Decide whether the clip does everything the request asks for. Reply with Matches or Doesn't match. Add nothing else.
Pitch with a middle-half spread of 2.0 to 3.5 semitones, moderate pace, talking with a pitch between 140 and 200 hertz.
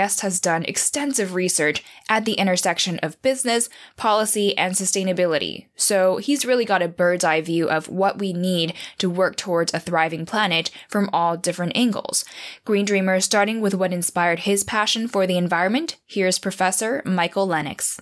Matches